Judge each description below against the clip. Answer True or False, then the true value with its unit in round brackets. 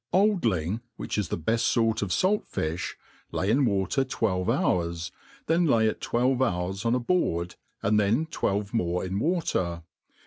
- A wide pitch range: True (6.2 semitones)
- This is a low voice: True (105 Hz)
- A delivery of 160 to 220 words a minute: True (170 wpm)